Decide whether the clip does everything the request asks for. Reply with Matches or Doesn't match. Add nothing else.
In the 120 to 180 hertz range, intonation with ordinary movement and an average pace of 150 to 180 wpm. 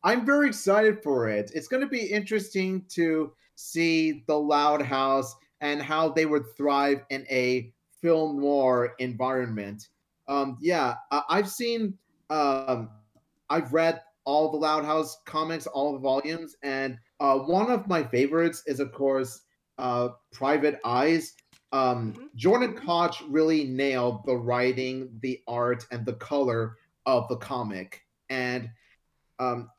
Doesn't match